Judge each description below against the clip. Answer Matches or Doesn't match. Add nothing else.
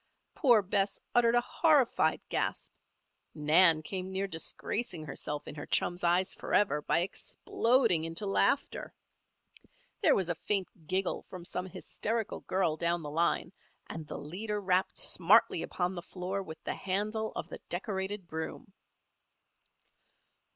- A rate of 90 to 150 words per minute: Matches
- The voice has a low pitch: Doesn't match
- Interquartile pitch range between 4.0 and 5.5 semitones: Doesn't match